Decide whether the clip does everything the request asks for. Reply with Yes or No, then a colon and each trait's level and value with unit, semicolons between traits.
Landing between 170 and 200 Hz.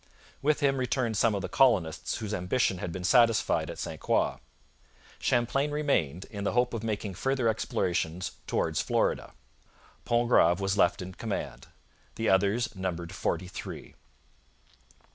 No: low, 105 Hz